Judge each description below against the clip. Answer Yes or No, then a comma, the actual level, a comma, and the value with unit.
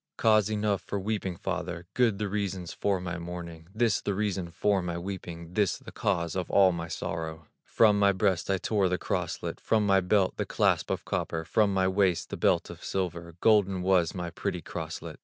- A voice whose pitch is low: Yes, very low, 95 Hz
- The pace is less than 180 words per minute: No, average, 195 wpm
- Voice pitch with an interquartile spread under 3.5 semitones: Yes, average, 2.9 semitones